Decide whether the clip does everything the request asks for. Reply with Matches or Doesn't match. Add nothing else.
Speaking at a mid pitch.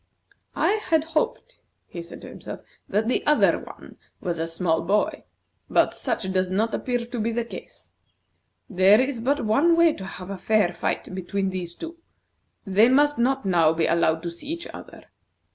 Doesn't match